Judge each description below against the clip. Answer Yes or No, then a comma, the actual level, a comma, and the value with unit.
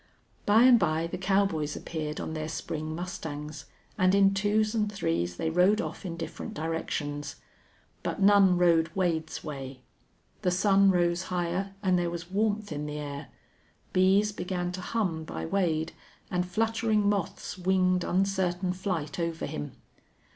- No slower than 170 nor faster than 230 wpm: No, average, 150 wpm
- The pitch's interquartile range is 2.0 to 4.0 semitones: Yes, average, 3.6 semitones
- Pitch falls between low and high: Yes, medium, 180 Hz